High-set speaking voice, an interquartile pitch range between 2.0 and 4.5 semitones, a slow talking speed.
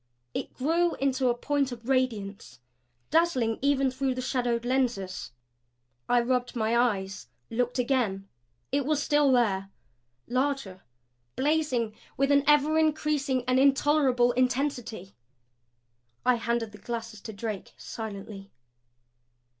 Yes: very high, 250 Hz; average, 3.5 semitones; slow, 120 wpm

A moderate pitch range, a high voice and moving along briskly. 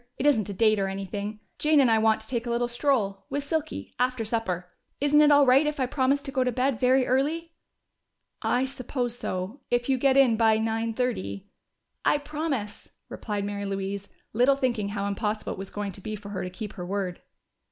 Yes: average, 4.8 semitones; high, 235 Hz; fast, 215 wpm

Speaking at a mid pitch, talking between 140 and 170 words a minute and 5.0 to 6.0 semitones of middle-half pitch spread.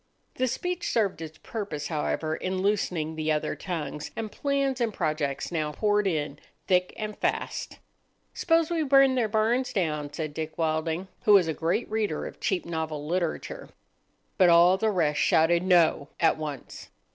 Yes: medium, 175 Hz; average, 165 wpm; wide, 5.5 semitones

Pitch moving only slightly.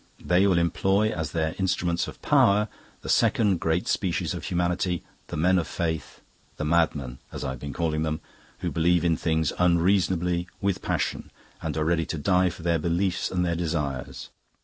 Yes: narrow, 2.1 semitones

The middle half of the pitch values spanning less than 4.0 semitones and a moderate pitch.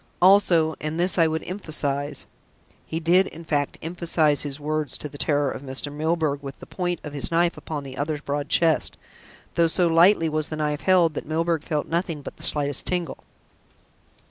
Yes: narrow, 2.5 semitones; medium, 155 Hz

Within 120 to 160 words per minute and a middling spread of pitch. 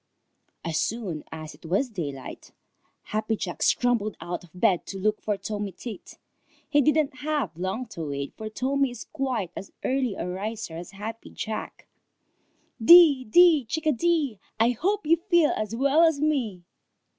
No: average, 155 wpm; wide, 6.9 semitones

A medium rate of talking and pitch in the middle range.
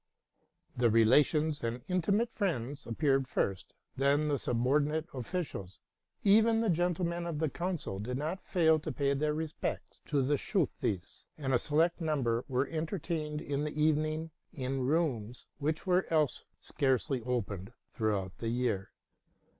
Yes: average, 145 wpm; medium, 145 Hz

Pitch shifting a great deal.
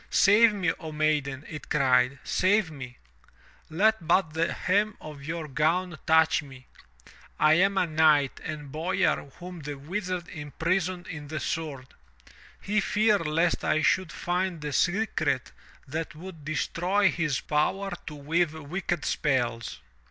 No: average, 3.8 semitones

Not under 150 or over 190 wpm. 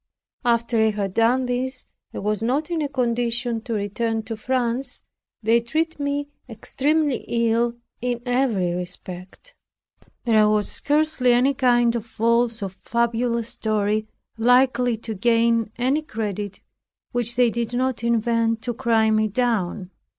No: average, 140 wpm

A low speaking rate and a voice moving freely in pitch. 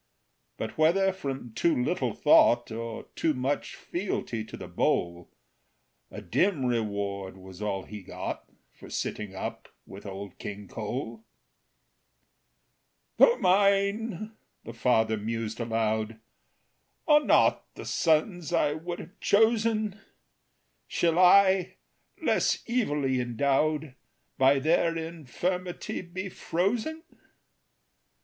Yes: slow, 110 wpm; wide, 8.9 semitones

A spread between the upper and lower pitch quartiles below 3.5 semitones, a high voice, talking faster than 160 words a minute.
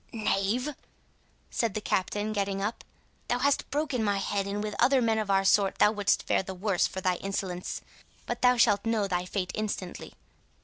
Yes: narrow, 2.6 semitones; high, 205 Hz; average, 185 wpm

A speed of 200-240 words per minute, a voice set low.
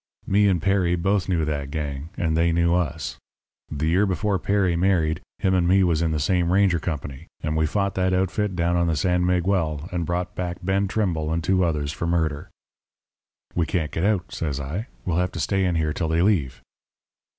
Yes: fast, 205 wpm; very low, 85 Hz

